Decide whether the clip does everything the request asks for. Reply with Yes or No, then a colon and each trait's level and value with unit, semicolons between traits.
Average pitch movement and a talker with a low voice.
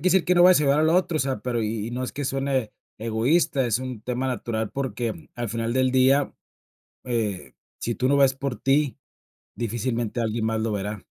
Yes: average, 3.5 semitones; low, 125 Hz